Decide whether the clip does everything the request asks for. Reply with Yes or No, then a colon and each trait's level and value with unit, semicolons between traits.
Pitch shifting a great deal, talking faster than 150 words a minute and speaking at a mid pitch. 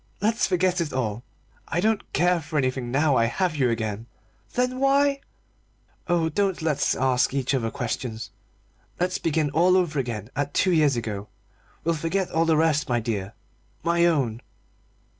Yes: wide, 6.3 semitones; average, 165 wpm; medium, 150 Hz